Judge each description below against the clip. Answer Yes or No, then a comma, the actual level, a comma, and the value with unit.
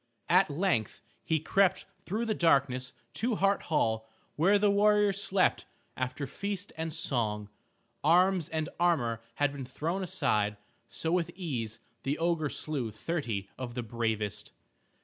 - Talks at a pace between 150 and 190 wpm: No, average, 140 wpm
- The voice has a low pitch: No, medium, 155 Hz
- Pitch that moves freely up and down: Yes, wide, 7.4 semitones